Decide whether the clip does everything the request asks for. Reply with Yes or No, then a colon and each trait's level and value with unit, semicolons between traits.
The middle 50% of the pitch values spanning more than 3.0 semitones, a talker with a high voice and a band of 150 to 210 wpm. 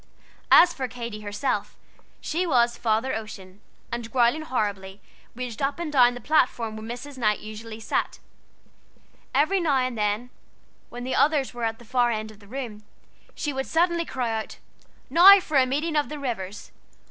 Yes: average, 4.7 semitones; high, 245 Hz; average, 170 wpm